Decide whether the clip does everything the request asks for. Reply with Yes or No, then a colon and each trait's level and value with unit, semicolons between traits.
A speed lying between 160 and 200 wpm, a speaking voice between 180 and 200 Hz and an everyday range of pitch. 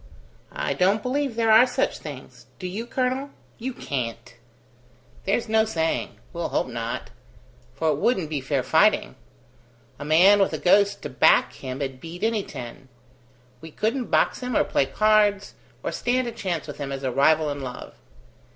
No: average, 170 wpm; medium, 185 Hz; wide, 8.2 semitones